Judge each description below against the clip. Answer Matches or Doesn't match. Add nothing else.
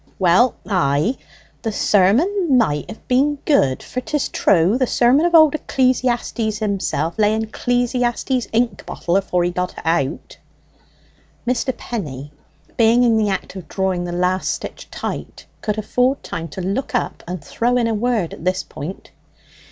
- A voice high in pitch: Matches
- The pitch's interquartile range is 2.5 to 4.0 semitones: Doesn't match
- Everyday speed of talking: Matches